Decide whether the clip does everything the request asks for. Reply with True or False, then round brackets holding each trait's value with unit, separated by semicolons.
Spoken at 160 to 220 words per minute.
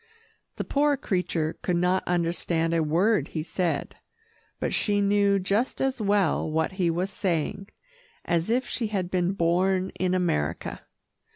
False (150 wpm)